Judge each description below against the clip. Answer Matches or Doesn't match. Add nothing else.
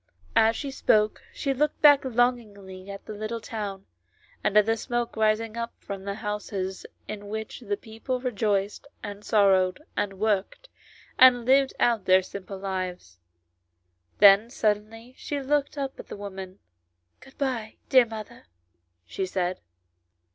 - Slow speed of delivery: Doesn't match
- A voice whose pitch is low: Doesn't match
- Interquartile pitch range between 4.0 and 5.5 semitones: Doesn't match